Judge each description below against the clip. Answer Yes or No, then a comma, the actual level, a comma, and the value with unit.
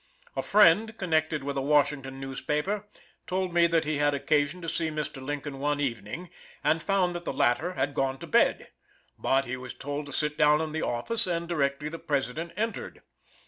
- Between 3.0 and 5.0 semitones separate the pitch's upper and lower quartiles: Yes, average, 3.6 semitones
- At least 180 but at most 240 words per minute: Yes, average, 190 wpm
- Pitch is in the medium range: Yes, medium, 150 Hz